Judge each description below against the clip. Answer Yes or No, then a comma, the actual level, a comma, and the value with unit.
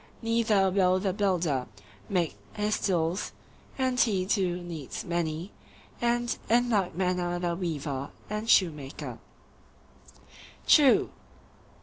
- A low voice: No, medium, 185 Hz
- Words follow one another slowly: Yes, slow, 100 wpm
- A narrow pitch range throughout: No, average, 3.8 semitones